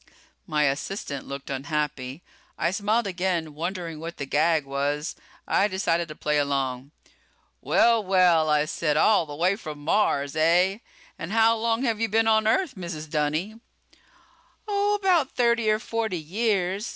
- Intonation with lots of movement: Yes, wide, 6.4 semitones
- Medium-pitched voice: Yes, medium, 175 Hz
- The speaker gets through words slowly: No, average, 150 wpm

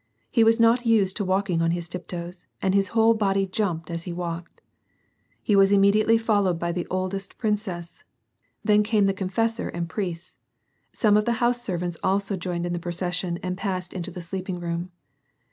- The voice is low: No, high, 190 Hz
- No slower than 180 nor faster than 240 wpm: Yes, average, 190 wpm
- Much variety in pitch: No, average, 3.2 semitones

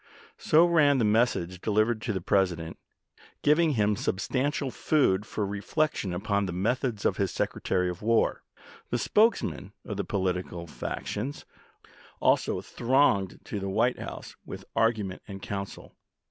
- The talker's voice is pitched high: No, low, 105 Hz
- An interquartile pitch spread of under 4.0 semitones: No, average, 5.1 semitones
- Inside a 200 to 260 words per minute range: No, average, 145 wpm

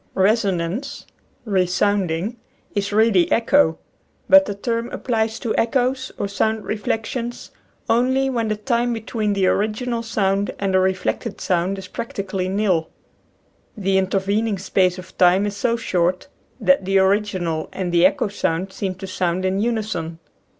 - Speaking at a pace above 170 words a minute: No, average, 150 wpm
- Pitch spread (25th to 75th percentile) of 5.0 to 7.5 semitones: No, average, 3.4 semitones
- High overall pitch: Yes, high, 200 Hz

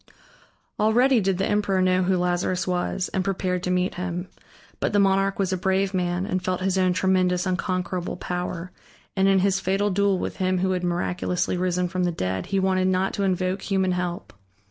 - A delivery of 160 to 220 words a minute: Yes, average, 195 wpm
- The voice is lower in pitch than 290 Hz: Yes, medium, 185 Hz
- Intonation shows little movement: Yes, narrow, 1.2 semitones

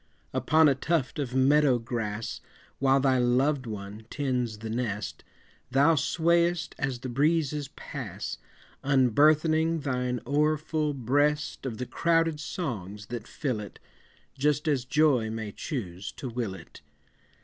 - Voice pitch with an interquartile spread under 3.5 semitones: No, average, 4.1 semitones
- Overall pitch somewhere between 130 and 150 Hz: Yes, low, 135 Hz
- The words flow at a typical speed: No, slow, 130 wpm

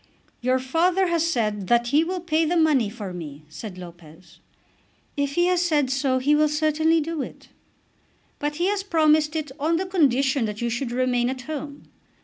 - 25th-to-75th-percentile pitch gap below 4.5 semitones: No, average, 5.3 semitones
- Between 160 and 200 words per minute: Yes, average, 185 wpm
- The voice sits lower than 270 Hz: No, very high, 285 Hz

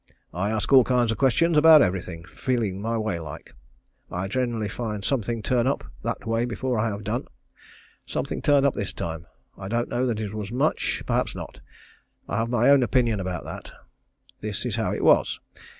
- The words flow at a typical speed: Yes, average, 195 wpm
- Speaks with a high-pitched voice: No, low, 115 Hz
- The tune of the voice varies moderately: Yes, average, 3.8 semitones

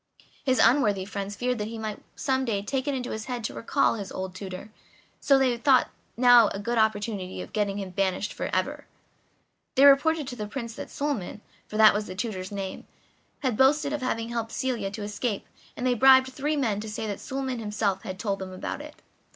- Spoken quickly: Yes, fast, 215 wpm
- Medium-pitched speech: No, high, 225 Hz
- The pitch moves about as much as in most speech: Yes, average, 4.4 semitones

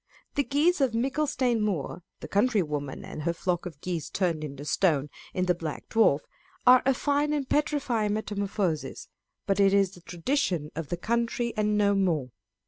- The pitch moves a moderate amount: No, wide, 6.5 semitones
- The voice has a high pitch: Yes, high, 200 Hz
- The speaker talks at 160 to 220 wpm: Yes, average, 175 wpm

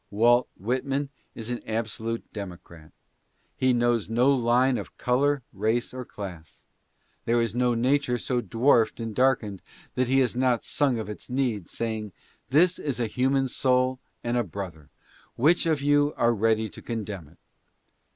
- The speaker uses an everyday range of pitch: Yes, average, 3.0 semitones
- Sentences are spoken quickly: No, average, 160 wpm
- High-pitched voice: No, low, 120 Hz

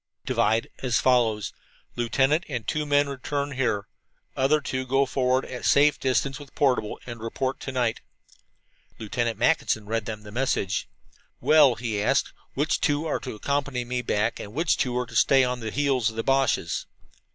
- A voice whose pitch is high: No, low, 125 Hz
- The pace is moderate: Yes, average, 175 wpm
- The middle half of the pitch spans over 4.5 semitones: No, average, 3.4 semitones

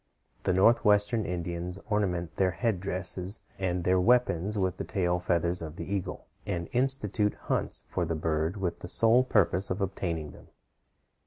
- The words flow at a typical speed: Yes, average, 155 wpm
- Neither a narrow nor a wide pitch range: Yes, average, 3.0 semitones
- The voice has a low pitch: Yes, very low, 90 Hz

